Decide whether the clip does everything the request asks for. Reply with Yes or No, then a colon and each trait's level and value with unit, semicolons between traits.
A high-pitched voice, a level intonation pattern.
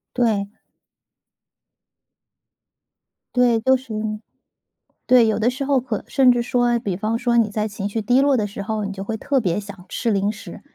No: high, 225 Hz; average, 3.1 semitones